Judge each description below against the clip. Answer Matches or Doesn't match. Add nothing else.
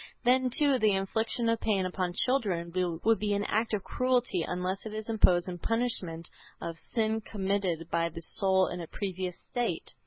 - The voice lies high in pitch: Matches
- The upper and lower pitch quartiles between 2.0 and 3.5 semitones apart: Doesn't match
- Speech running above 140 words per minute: Matches